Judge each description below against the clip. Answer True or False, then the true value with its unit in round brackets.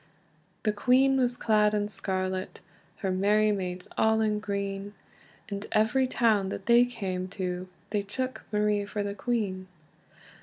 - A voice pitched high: True (205 Hz)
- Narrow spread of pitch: True (2.3 semitones)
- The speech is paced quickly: False (145 wpm)